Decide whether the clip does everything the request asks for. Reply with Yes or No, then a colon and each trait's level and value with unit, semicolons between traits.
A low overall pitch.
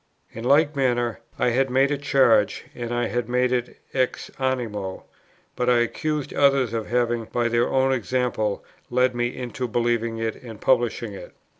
Yes: low, 120 Hz